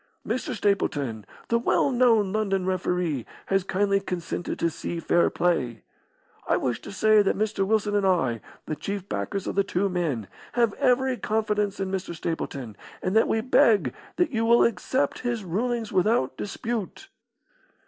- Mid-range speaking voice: No, high, 200 Hz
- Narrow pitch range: No, average, 4.1 semitones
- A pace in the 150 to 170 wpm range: Yes, average, 160 wpm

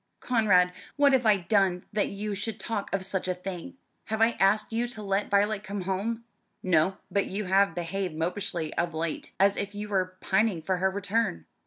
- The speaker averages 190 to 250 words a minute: Yes, average, 195 wpm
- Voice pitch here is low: No, high, 195 Hz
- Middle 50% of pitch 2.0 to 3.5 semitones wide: Yes, narrow, 2.5 semitones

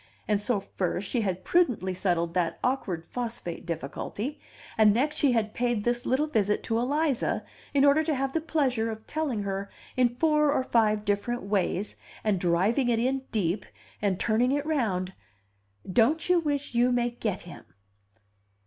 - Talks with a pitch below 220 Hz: No, high, 230 Hz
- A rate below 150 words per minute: No, average, 165 wpm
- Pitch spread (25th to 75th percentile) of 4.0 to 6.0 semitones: Yes, average, 5.2 semitones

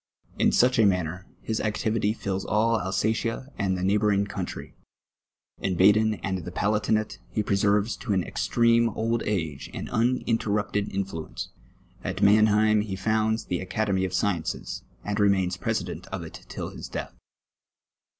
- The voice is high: No, low, 105 Hz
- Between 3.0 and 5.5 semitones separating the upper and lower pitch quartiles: No, narrow, 2.5 semitones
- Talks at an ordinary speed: Yes, average, 150 wpm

